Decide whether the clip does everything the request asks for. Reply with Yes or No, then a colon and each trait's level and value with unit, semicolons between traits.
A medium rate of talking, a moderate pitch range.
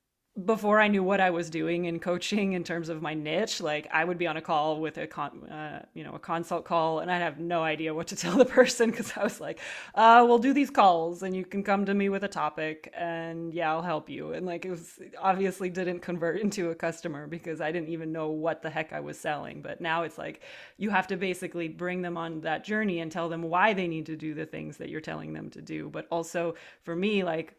No: fast, 260 wpm; average, 3.0 semitones